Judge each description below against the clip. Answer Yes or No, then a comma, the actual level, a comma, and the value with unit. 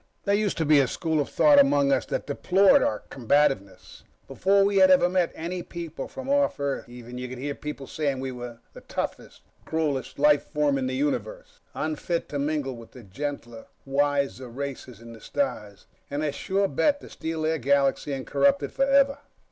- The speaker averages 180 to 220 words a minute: Yes, average, 190 wpm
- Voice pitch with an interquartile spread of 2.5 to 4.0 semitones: No, average, 5.2 semitones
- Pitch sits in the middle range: Yes, medium, 145 Hz